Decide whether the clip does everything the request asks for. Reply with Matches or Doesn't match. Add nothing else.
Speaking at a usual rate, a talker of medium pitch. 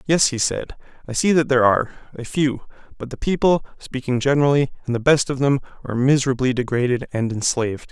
Doesn't match